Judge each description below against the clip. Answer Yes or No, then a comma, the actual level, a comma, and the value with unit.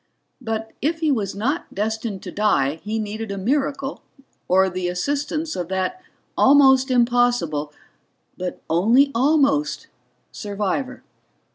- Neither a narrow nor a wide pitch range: No, wide, 6.3 semitones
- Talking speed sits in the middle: No, slow, 120 wpm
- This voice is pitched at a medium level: No, high, 225 Hz